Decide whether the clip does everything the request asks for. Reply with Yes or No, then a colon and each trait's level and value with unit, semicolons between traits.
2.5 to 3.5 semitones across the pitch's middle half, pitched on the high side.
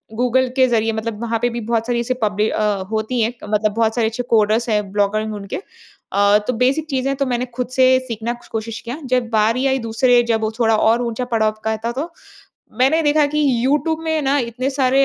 Yes: average, 2.9 semitones; high, 235 Hz